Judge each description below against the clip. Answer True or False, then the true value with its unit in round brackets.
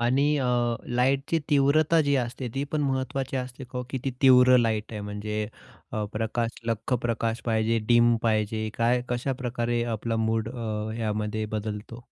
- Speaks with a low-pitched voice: True (120 Hz)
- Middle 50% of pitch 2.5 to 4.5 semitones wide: True (2.8 semitones)